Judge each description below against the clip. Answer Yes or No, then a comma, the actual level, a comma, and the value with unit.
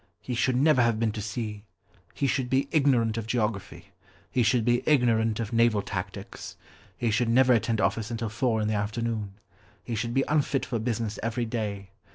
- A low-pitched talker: Yes, low, 115 Hz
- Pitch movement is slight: Yes, narrow, 2.3 semitones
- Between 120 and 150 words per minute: No, average, 190 wpm